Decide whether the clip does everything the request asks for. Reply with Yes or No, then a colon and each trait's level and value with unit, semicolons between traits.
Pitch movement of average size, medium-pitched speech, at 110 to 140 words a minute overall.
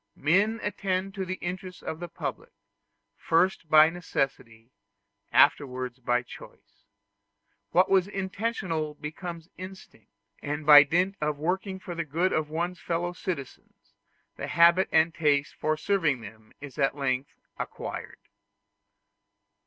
Yes: average, 4.2 semitones; medium, 165 Hz; slow, 135 wpm